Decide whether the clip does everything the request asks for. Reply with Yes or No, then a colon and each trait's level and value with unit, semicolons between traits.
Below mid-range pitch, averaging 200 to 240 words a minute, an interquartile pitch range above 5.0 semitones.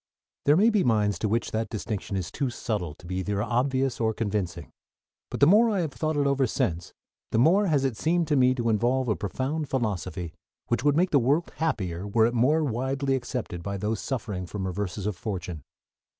Yes: low, 120 Hz; fast, 205 wpm; wide, 5.6 semitones